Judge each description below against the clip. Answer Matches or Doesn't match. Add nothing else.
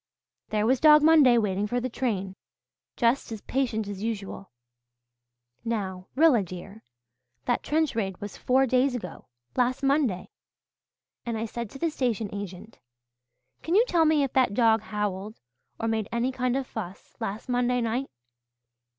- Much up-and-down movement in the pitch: Doesn't match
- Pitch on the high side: Matches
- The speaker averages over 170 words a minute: Doesn't match